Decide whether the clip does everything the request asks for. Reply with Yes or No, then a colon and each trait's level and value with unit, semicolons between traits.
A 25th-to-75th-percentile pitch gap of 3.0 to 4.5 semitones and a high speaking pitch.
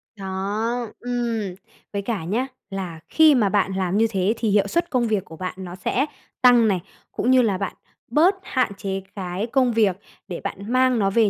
Yes: average, 4.1 semitones; high, 210 Hz